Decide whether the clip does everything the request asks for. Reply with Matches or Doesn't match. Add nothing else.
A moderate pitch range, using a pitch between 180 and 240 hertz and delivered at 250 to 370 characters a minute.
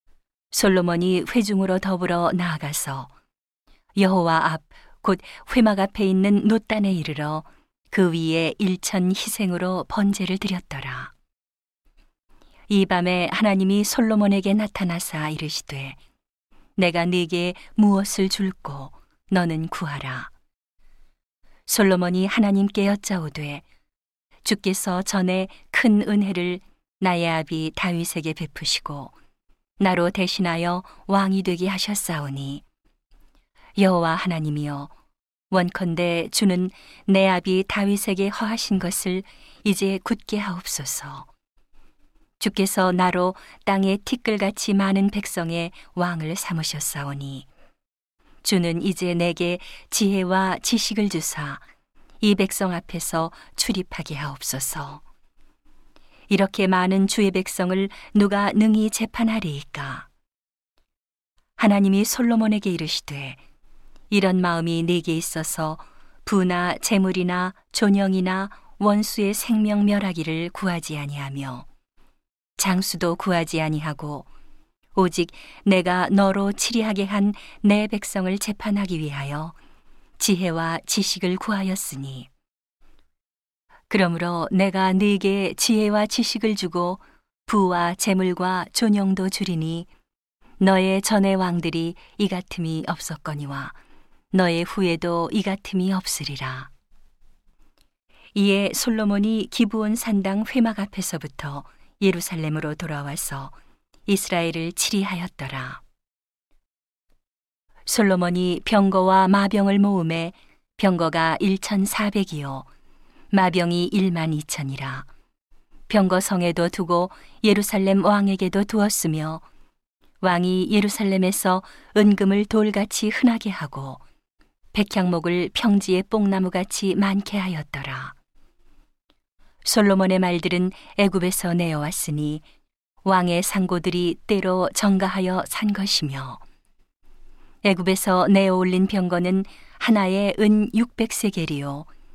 Doesn't match